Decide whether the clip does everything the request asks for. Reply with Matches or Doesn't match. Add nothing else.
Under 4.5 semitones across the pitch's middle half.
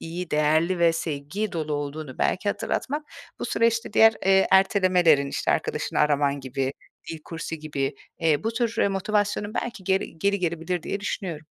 Doesn't match